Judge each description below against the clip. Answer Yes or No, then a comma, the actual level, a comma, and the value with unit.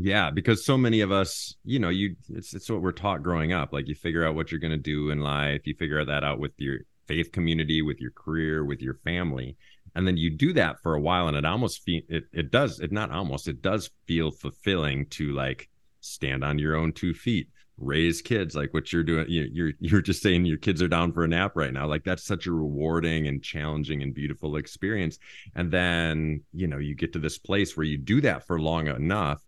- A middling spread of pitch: Yes, average, 3.2 semitones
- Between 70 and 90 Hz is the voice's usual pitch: Yes, very low, 80 Hz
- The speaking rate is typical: No, fast, 235 wpm